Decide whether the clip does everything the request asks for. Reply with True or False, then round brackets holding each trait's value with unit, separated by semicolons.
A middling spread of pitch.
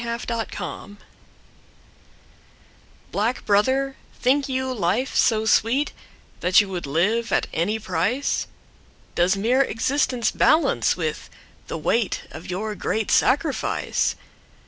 True (4.8 semitones)